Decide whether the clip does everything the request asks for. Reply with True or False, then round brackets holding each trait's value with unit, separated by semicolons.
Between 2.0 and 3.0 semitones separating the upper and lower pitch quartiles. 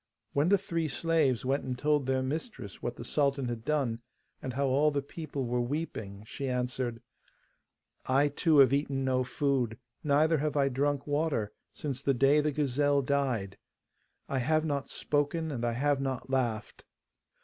True (2.7 semitones)